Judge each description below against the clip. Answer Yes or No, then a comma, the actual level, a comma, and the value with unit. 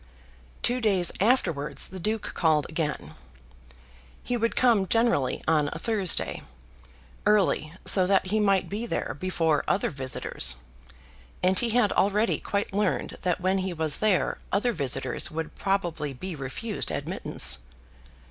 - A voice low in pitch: No, medium, 185 Hz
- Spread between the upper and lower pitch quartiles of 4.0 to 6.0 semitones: Yes, average, 5.0 semitones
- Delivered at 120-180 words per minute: Yes, average, 140 wpm